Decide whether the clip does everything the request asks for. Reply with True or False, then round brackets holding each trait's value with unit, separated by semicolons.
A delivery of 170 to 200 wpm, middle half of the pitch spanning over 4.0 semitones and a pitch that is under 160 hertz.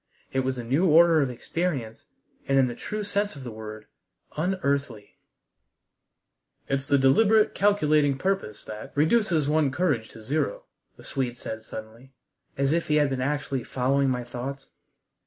False (155 wpm; 4.6 semitones; 140 Hz)